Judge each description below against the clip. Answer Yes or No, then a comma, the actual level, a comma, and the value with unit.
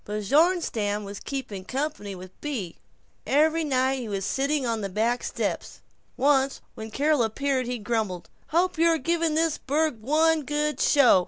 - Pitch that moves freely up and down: Yes, wide, 5.9 semitones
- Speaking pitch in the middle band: No, very high, 265 Hz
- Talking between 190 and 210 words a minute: No, average, 165 wpm